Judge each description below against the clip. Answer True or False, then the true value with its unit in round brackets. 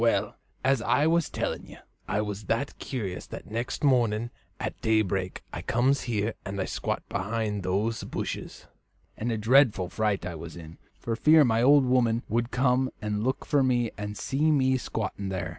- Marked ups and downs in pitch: False (3.9 semitones)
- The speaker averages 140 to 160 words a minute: False (175 wpm)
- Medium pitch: False (115 Hz)